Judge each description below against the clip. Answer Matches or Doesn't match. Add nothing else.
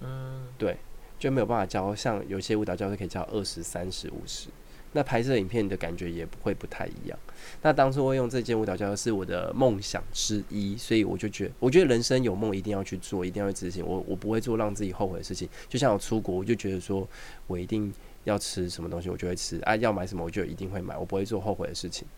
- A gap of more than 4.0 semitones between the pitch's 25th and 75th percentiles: Doesn't match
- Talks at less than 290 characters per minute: Doesn't match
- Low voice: Matches